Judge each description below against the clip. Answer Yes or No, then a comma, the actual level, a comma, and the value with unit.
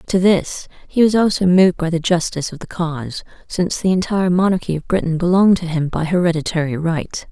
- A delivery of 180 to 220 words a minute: Yes, average, 195 wpm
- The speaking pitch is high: No, medium, 175 Hz